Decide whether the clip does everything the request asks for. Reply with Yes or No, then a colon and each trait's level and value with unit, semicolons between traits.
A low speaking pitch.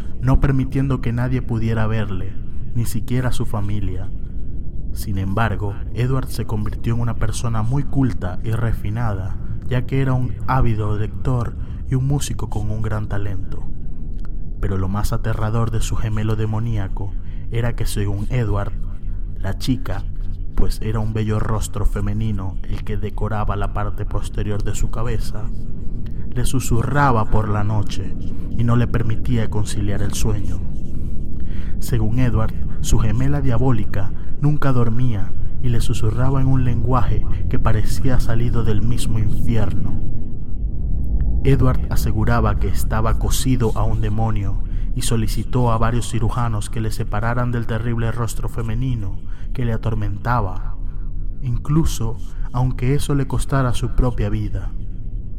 Yes: low, 110 Hz